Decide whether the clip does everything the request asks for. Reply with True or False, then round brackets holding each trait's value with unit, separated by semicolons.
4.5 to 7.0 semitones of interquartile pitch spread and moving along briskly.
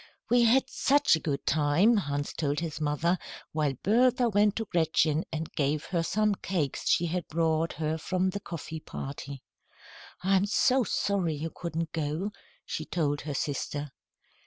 False (4.8 semitones; 160 wpm)